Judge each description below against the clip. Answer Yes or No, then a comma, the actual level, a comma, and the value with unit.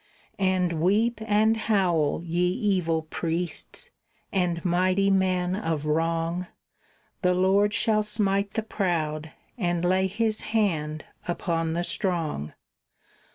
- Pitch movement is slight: No, average, 3.3 semitones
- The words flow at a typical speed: No, slow, 110 wpm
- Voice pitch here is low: No, medium, 180 Hz